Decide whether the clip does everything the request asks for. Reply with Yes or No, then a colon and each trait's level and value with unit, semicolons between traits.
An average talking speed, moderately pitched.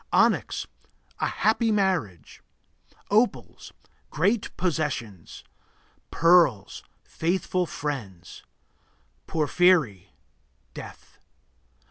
No: slow, 60 wpm; medium, 160 Hz